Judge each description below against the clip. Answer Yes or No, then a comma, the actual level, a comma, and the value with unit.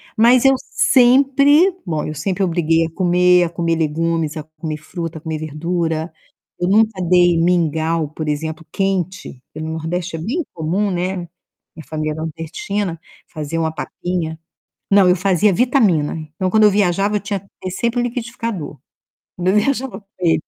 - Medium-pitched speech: Yes, medium, 175 Hz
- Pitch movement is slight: No, average, 4.0 semitones